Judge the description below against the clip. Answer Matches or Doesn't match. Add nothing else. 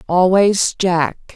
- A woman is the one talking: Matches